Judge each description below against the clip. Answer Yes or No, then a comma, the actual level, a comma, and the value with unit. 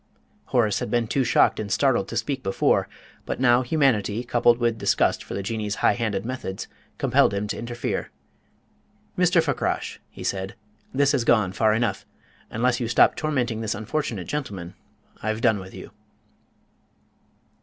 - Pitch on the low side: Yes, low, 115 Hz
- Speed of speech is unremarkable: Yes, average, 155 wpm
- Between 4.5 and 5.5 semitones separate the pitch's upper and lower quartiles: No, average, 3.2 semitones